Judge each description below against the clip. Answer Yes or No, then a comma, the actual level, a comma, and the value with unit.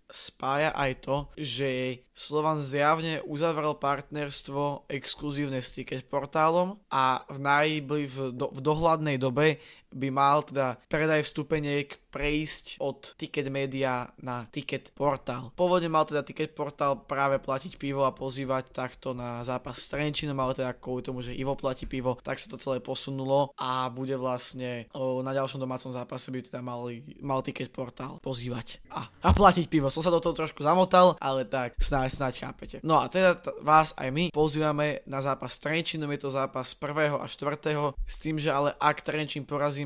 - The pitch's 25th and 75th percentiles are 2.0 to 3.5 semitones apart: Yes, narrow, 2.5 semitones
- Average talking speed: No, fast, 170 wpm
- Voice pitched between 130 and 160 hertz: Yes, medium, 140 Hz